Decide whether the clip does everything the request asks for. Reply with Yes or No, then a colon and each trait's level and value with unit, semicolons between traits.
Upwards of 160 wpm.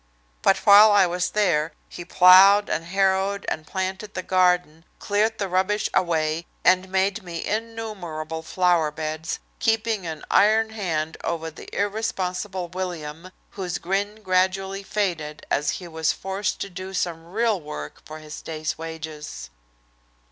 No: average, 140 wpm